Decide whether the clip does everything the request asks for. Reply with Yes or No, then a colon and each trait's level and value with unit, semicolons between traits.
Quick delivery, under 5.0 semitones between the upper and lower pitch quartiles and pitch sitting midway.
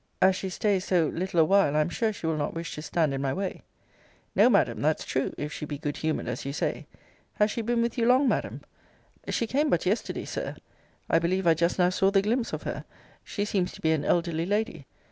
Yes: fast, 240 wpm; average, 4.6 semitones; medium, 180 Hz